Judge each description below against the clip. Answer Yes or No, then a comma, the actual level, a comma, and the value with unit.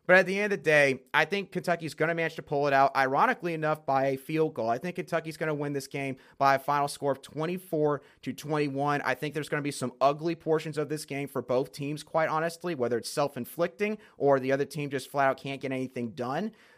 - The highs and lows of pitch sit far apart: No, average, 3.0 semitones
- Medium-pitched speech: Yes, medium, 145 Hz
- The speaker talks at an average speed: No, fast, 240 wpm